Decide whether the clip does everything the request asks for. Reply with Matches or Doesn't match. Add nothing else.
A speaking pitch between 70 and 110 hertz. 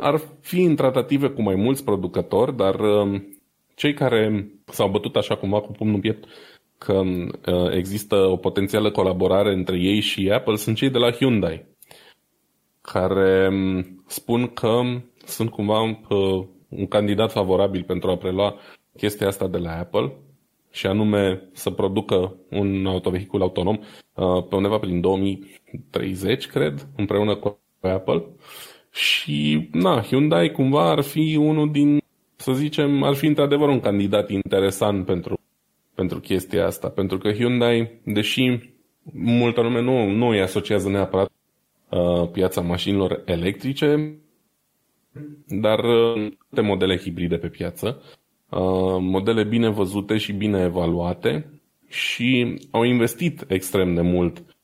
Matches